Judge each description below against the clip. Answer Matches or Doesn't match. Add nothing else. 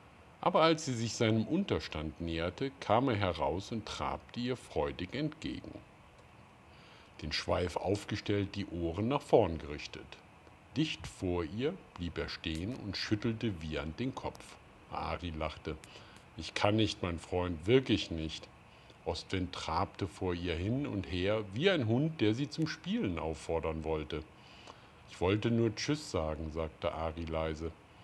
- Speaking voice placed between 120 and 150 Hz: Doesn't match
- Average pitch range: Doesn't match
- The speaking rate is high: Doesn't match